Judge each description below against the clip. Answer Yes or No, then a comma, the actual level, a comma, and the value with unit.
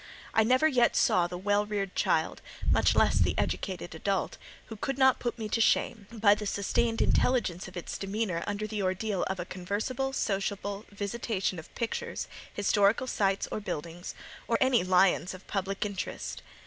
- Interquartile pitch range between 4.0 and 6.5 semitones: No, average, 3.2 semitones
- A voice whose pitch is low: No, high, 205 Hz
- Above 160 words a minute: Yes, average, 170 wpm